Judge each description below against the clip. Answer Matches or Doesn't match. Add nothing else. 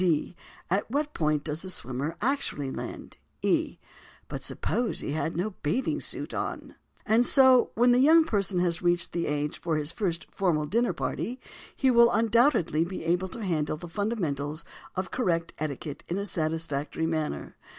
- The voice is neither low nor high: Matches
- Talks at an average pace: Matches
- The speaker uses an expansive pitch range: Matches